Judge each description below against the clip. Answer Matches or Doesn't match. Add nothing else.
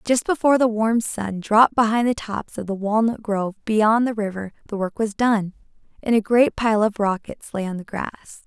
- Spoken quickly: Matches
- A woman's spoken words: Matches